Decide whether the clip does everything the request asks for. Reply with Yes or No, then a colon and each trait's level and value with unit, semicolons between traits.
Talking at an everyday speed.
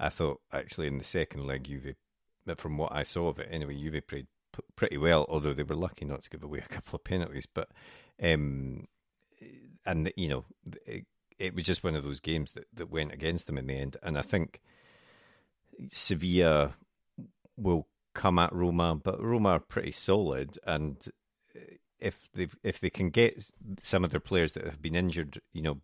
Yes: average, 195 wpm